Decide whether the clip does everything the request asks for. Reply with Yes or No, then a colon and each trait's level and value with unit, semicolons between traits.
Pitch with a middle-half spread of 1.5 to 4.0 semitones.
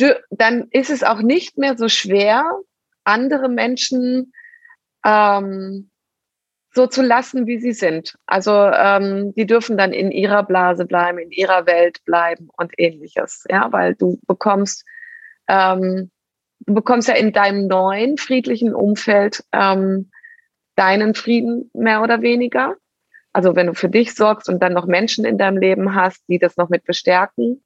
No: average, 4.6 semitones